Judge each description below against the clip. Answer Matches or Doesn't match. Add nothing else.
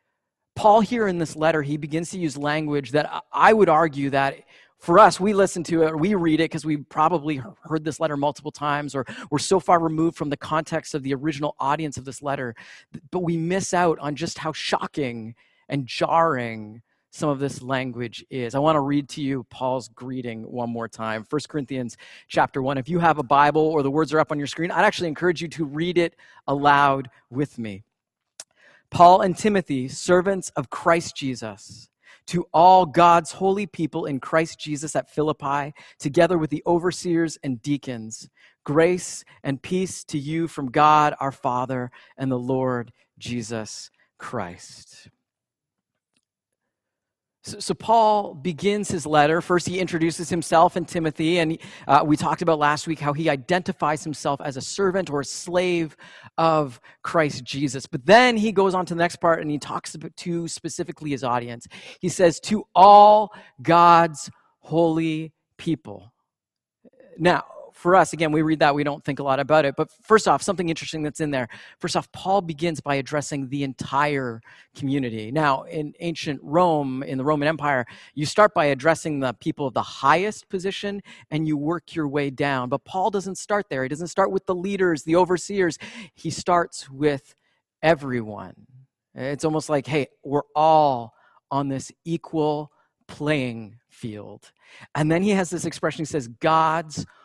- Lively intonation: Doesn't match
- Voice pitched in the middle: Matches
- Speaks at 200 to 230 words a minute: Doesn't match